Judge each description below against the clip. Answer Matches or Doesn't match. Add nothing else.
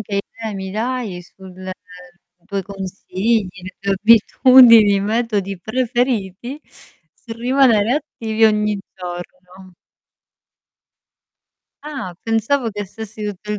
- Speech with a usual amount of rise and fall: Matches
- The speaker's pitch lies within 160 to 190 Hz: Doesn't match